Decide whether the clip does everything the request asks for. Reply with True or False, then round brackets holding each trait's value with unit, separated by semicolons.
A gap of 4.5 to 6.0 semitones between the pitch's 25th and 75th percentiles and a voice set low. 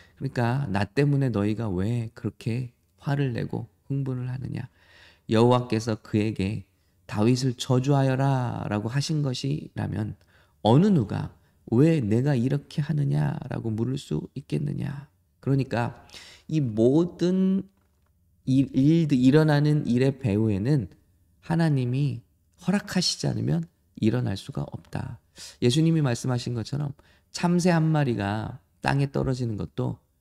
True (5.4 semitones; 125 Hz)